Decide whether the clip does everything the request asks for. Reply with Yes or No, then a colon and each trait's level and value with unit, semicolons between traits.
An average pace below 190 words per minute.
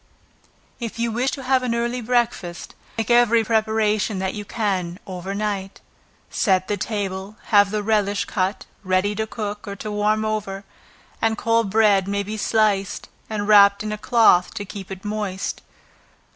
Yes: average, 165 wpm